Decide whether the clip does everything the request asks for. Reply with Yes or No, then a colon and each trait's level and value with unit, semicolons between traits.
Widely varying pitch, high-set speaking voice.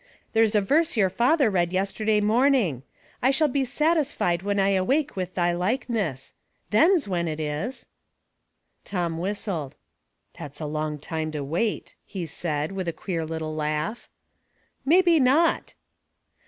Yes: wide, 7.6 semitones; high, 195 Hz